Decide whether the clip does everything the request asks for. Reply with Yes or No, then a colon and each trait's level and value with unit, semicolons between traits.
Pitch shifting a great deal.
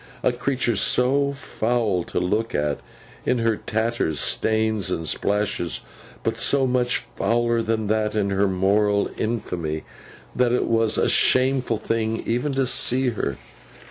No: average, 3.3 semitones